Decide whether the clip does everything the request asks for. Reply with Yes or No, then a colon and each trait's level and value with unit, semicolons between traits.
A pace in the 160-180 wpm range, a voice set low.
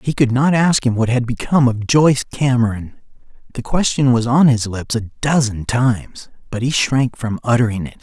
No: average, 195 wpm; low, 125 Hz